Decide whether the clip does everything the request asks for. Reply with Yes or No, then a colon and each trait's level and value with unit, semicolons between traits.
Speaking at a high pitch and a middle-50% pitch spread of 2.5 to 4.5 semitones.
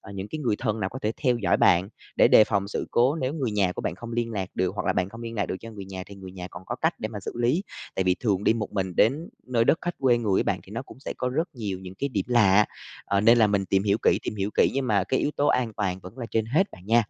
No: low, 105 Hz; average, 3.9 semitones